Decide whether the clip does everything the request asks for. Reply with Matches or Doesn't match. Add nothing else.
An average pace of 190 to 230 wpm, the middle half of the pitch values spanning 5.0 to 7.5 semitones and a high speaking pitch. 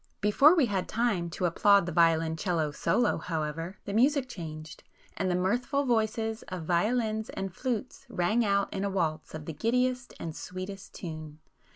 Doesn't match